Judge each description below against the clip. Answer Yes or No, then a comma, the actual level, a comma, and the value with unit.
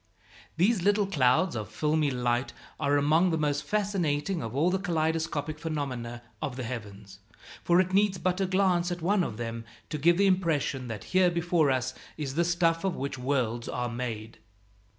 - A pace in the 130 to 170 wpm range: No, average, 180 wpm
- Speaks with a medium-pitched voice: Yes, medium, 155 Hz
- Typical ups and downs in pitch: No, wide, 5.9 semitones